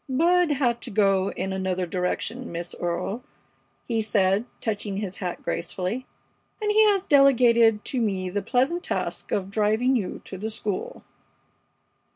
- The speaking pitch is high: Yes, high, 215 Hz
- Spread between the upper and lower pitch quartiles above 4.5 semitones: Yes, average, 5.0 semitones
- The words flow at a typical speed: Yes, average, 150 wpm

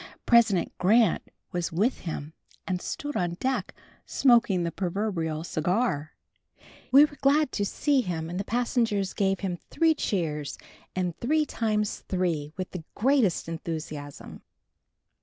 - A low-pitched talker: No, high, 190 Hz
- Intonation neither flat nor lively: No, wide, 6.1 semitones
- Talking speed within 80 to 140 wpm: Yes, slow, 135 wpm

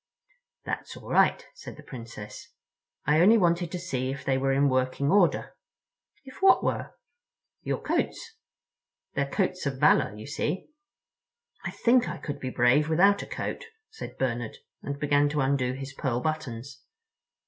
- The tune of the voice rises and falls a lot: Yes, wide, 5.7 semitones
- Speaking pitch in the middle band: Yes, medium, 145 Hz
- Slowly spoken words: No, average, 160 wpm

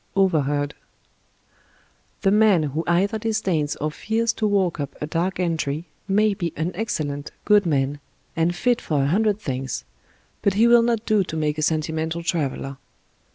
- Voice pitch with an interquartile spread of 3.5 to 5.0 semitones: No, wide, 5.6 semitones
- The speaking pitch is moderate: Yes, medium, 170 Hz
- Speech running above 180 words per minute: No, average, 160 wpm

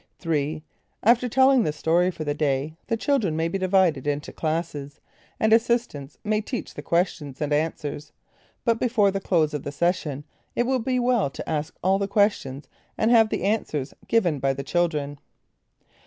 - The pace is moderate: Yes, average, 175 wpm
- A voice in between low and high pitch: Yes, medium, 170 Hz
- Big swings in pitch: Yes, wide, 6.7 semitones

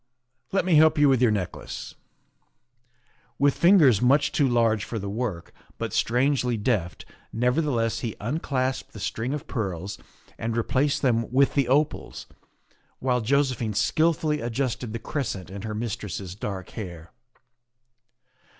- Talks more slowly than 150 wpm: Yes, average, 140 wpm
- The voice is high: No, low, 120 Hz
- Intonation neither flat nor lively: Yes, average, 4.5 semitones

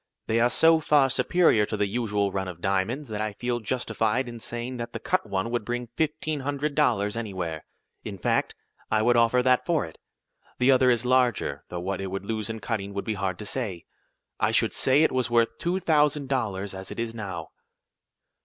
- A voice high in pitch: No, low, 115 Hz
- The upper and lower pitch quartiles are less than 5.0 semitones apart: Yes, average, 4.5 semitones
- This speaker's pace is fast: Yes, fast, 210 wpm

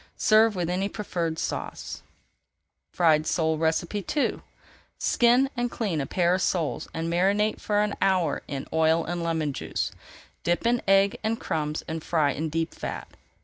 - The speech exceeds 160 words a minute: No, average, 155 wpm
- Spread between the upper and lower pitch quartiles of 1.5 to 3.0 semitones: No, average, 4.3 semitones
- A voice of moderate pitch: Yes, medium, 175 Hz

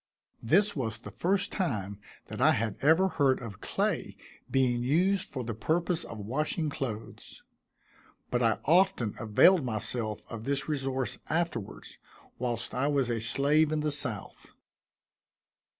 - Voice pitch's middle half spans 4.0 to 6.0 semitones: Yes, wide, 5.6 semitones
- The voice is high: No, low, 135 Hz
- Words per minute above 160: No, average, 140 wpm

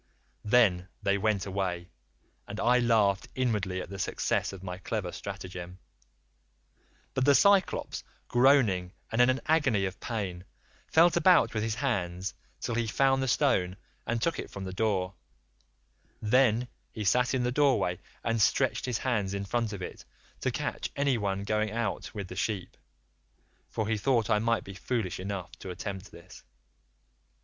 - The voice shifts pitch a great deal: No, average, 4.4 semitones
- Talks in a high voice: No, low, 105 Hz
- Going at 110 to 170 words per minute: Yes, average, 160 wpm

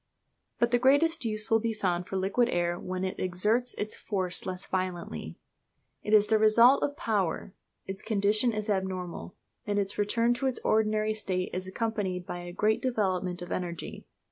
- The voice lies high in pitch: Yes, high, 205 Hz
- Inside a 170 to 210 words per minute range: Yes, average, 175 wpm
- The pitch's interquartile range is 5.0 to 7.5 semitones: No, average, 3.3 semitones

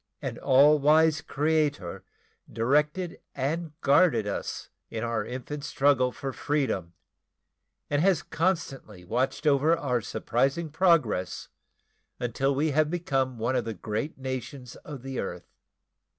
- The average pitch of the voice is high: No, medium, 140 Hz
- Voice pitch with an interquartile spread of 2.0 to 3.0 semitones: No, average, 3.8 semitones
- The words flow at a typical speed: No, slow, 125 wpm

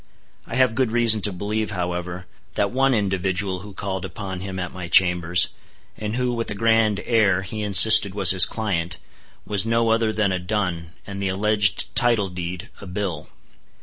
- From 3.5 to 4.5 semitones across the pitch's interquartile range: No, average, 3.1 semitones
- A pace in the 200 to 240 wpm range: No, average, 180 wpm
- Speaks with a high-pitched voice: No, low, 100 Hz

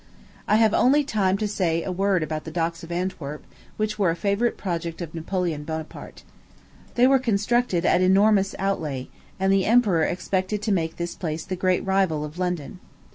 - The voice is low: No, medium, 185 Hz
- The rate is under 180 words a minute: No, average, 190 wpm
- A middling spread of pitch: Yes, average, 3.4 semitones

